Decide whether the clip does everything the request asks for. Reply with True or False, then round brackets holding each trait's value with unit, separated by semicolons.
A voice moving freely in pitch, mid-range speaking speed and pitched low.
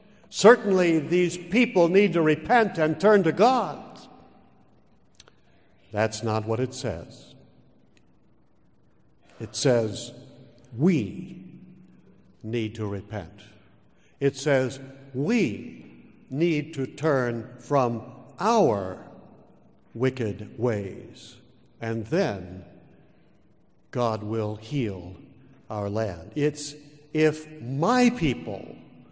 False (6.5 semitones; 85 wpm; 130 Hz)